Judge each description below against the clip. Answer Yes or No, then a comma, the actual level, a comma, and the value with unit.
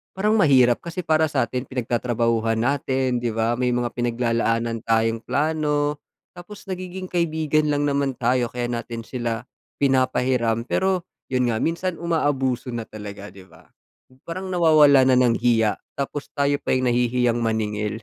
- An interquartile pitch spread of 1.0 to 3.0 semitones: No, average, 4.3 semitones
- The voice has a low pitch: Yes, low, 125 Hz